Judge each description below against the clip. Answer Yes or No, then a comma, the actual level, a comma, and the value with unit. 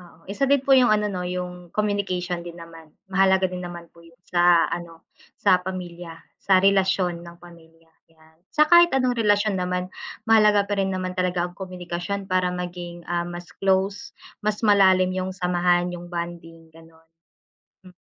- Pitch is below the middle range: No, medium, 180 Hz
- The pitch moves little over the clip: Yes, narrow, 2.2 semitones